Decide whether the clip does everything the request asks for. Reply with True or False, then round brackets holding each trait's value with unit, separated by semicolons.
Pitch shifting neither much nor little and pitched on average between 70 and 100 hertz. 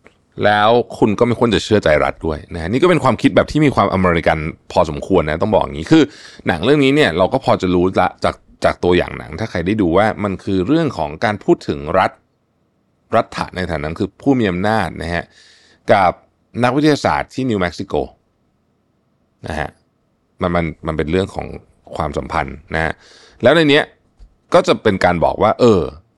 False (5.9 semitones; 95 Hz)